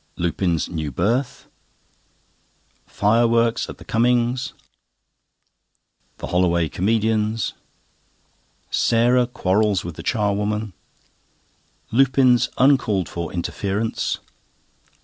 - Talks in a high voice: No, low, 110 Hz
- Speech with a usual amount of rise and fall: Yes, average, 4.5 semitones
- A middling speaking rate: No, slow, 75 wpm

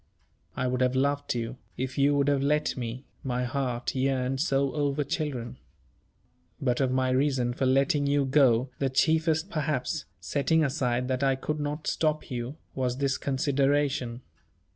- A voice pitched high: No, low, 135 Hz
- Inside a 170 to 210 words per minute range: No, average, 160 wpm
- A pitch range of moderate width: No, narrow, 2.2 semitones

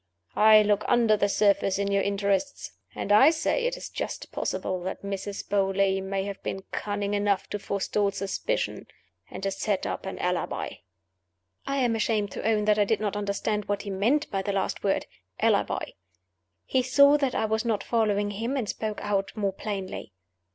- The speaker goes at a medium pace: Yes, average, 185 wpm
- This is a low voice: No, high, 205 Hz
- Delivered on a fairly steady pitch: Yes, narrow, 1.8 semitones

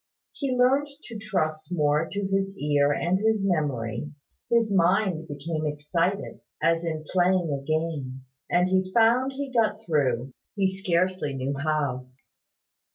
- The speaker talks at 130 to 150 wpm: Yes, average, 140 wpm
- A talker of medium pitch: Yes, medium, 170 Hz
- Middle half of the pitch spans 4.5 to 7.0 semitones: Yes, average, 5.0 semitones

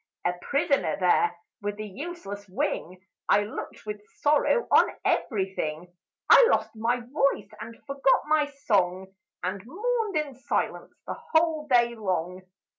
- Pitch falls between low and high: No, high, 230 Hz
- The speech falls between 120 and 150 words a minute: Yes, average, 140 wpm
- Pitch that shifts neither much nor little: No, wide, 7.6 semitones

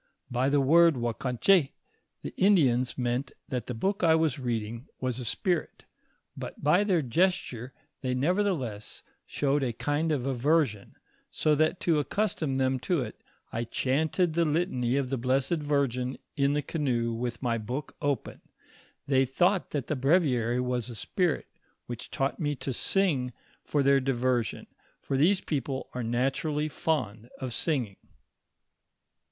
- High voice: No, low, 135 Hz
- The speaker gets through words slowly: No, average, 150 wpm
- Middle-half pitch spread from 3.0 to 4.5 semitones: Yes, average, 4.1 semitones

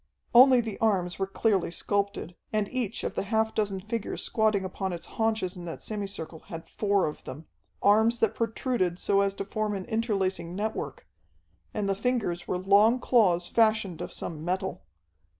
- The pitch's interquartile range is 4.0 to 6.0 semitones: No, average, 3.0 semitones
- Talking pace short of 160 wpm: No, average, 175 wpm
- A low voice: No, high, 200 Hz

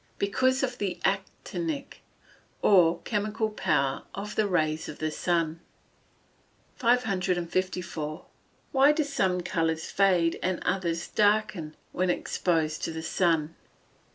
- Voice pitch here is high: No, medium, 180 Hz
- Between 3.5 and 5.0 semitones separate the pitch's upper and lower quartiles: Yes, average, 4.3 semitones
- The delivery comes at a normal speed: No, slow, 120 wpm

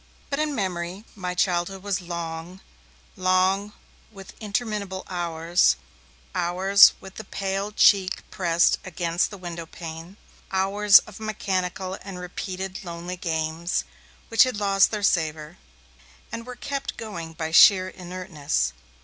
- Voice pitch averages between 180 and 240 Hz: Yes, medium, 185 Hz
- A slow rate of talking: Yes, slow, 125 wpm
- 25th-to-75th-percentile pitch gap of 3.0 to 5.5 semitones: No, narrow, 2.6 semitones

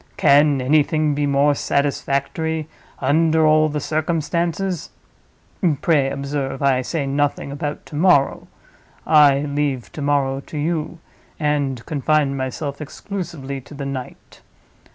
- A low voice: No, medium, 145 Hz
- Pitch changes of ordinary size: No, narrow, 2.0 semitones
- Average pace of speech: No, slow, 115 wpm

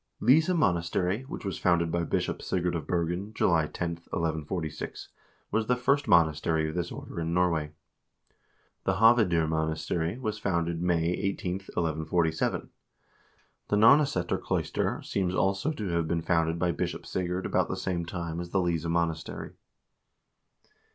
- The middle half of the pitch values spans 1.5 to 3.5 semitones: Yes, average, 2.8 semitones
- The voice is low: Yes, very low, 85 Hz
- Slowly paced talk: No, average, 150 wpm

